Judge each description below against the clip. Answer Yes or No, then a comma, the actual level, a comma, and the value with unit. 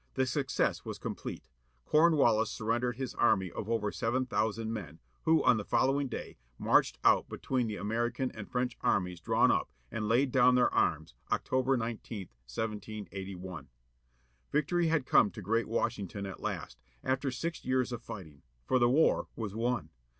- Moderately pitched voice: No, low, 115 Hz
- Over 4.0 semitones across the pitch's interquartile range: No, average, 3.7 semitones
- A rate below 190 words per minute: Yes, average, 160 wpm